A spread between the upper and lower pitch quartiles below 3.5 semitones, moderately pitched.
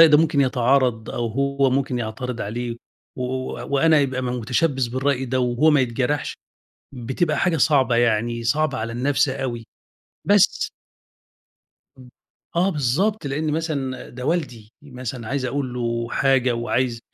No: average, 3.0 semitones; low, 130 Hz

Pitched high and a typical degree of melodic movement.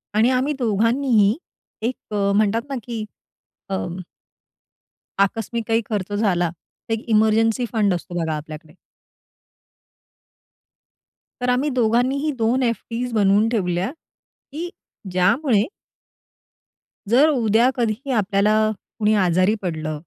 Yes: high, 220 Hz; average, 3.7 semitones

